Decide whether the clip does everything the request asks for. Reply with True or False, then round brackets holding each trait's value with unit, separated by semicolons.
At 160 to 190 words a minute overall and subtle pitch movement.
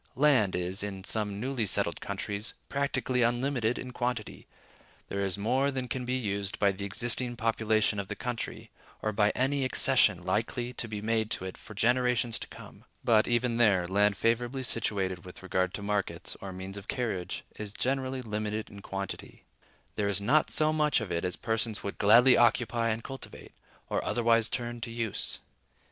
False (180 wpm; 3.5 semitones)